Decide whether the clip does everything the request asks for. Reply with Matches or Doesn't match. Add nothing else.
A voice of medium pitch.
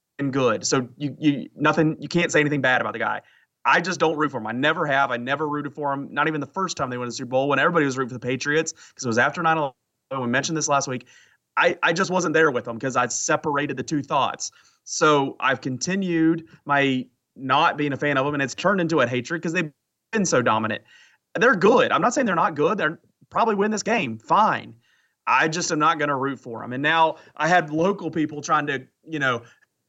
Matches